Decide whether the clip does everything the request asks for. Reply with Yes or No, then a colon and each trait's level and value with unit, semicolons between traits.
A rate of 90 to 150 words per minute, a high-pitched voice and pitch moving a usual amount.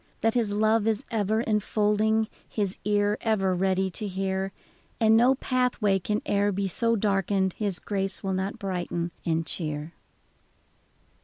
No: average, 145 wpm; high, 205 Hz; narrow, 2.3 semitones